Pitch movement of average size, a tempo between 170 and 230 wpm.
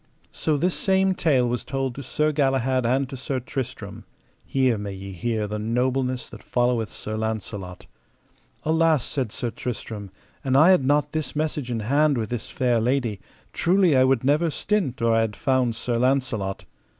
Yes: average, 3.9 semitones; average, 175 wpm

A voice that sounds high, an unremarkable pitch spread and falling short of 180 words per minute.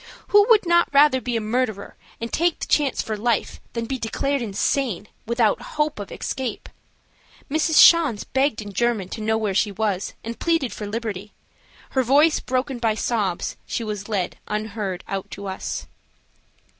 Yes: high, 230 Hz; average, 4.7 semitones; average, 170 wpm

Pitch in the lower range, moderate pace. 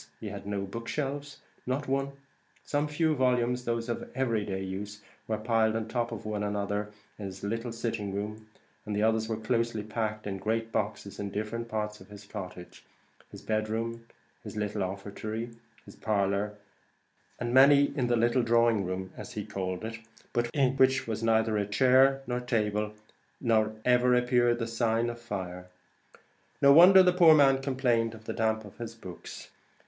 Yes: low, 115 Hz; average, 175 wpm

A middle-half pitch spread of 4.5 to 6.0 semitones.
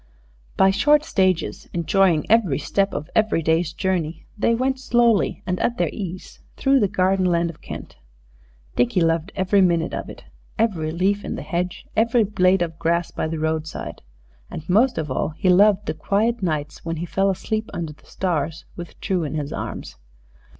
No: average, 4.0 semitones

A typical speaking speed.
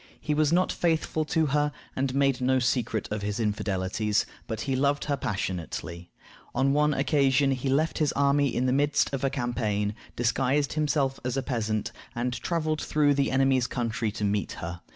Yes: average, 180 wpm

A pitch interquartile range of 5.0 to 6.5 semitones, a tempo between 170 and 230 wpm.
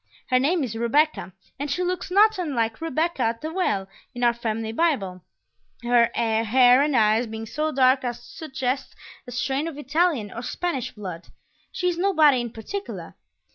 Yes: wide, 5.5 semitones; average, 175 wpm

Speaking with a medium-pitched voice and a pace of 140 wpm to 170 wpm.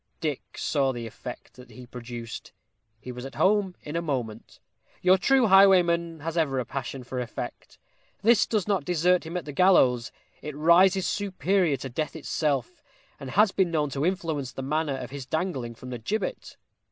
No: medium, 155 Hz; average, 180 wpm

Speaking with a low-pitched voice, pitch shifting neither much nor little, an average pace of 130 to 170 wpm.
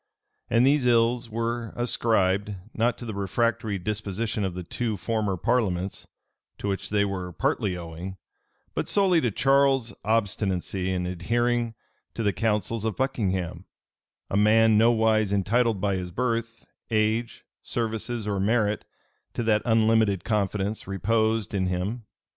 Yes: low, 110 Hz; average, 3.0 semitones; slow, 135 wpm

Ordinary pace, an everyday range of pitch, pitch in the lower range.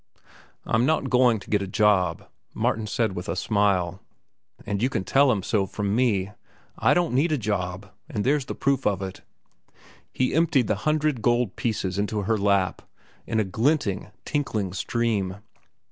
Yes: average, 170 wpm; average, 4.7 semitones; low, 105 Hz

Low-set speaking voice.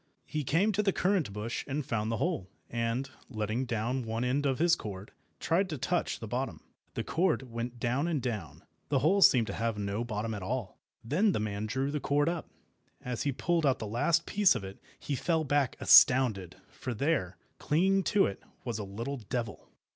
Yes: low, 125 Hz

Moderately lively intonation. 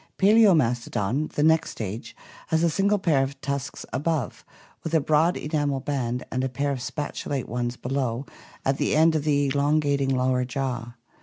Yes: average, 3.4 semitones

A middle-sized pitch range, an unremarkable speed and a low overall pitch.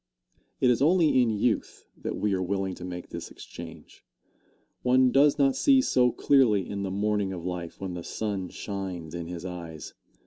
No: wide, 5.8 semitones; average, 180 wpm; low, 100 Hz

